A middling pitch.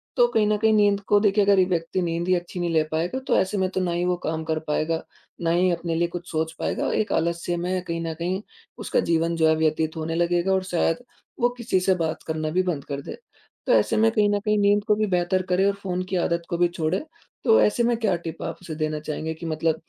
Yes: medium, 175 Hz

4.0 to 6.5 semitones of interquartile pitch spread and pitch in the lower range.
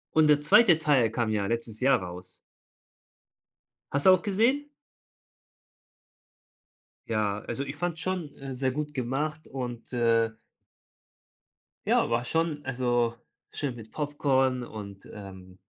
Yes: average, 4.6 semitones; low, 130 Hz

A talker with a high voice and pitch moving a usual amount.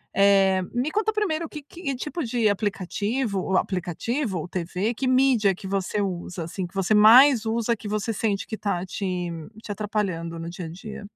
Yes: high, 205 Hz; average, 4.3 semitones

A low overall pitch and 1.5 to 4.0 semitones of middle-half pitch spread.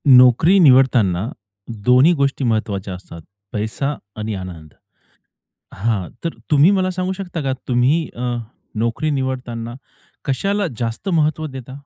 No: low, 130 Hz; wide, 5.6 semitones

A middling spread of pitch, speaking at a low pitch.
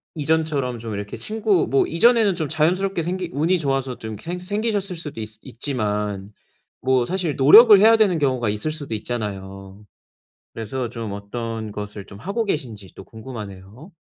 No: wide, 8.7 semitones; low, 130 Hz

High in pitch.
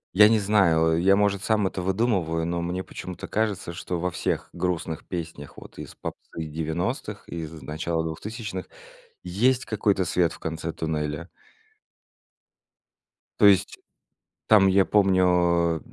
No: very low, 90 Hz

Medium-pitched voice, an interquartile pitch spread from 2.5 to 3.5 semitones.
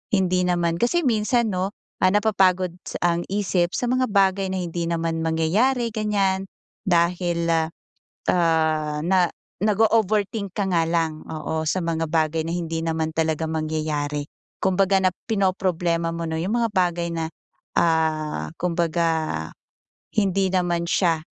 Yes: medium, 175 Hz; average, 3.0 semitones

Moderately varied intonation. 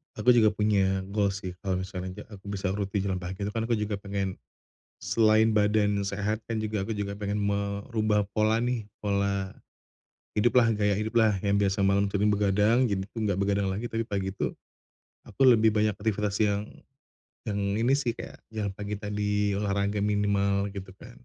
No: narrow, 1.4 semitones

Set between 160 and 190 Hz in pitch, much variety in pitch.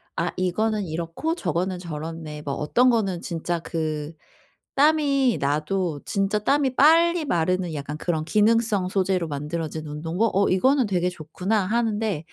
Yes: medium, 185 Hz; wide, 5.7 semitones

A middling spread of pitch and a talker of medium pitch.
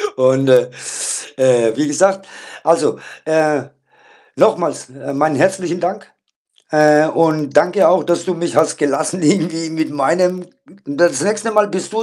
Yes: average, 3.7 semitones; medium, 160 Hz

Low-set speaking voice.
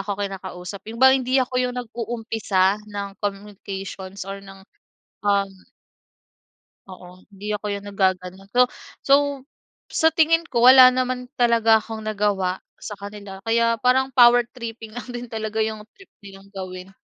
No: high, 210 Hz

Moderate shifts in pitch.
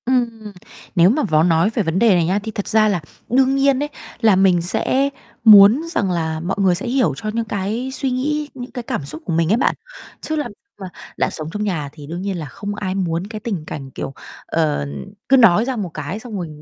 No: wide, 5.9 semitones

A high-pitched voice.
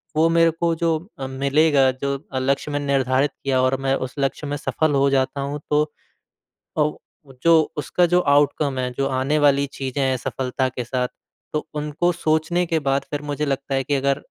No: medium, 140 Hz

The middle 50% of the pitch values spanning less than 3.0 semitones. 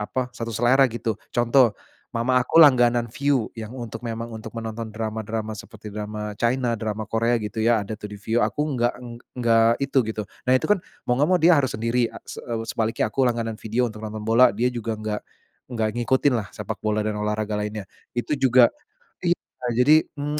Yes: narrow, 2.5 semitones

